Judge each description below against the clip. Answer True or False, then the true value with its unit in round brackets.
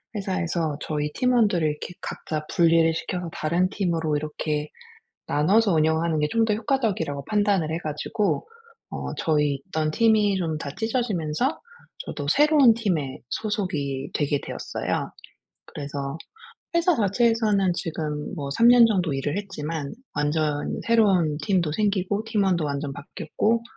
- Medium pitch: True (170 Hz)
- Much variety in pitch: True (6.0 semitones)